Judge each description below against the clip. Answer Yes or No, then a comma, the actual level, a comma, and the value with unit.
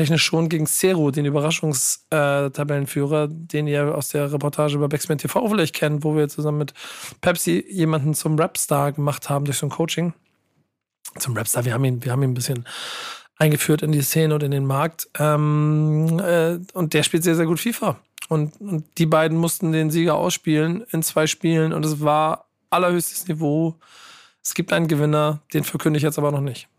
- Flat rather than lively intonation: Yes, narrow, 1.9 semitones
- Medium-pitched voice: Yes, medium, 155 Hz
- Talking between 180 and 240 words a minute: Yes, fast, 190 wpm